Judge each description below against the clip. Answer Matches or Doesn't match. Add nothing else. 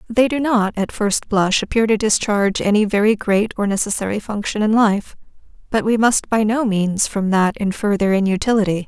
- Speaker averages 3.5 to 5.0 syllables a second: Doesn't match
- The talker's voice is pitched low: Doesn't match